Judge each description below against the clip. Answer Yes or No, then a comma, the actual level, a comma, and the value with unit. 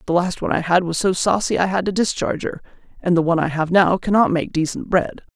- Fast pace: Yes, fast, 260 wpm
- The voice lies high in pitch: No, medium, 180 Hz